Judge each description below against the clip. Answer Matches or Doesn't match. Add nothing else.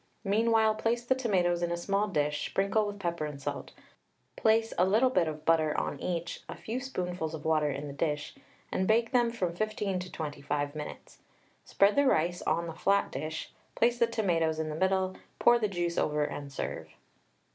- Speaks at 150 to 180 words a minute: Doesn't match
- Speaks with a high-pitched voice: Doesn't match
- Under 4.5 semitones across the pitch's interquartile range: Doesn't match